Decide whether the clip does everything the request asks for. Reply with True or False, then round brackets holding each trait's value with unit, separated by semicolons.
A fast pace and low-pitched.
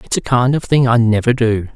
True (275 wpm; 120 Hz)